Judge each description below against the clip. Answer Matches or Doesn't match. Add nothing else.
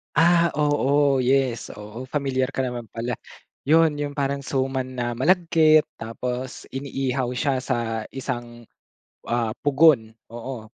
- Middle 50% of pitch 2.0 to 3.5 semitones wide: Matches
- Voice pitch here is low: Matches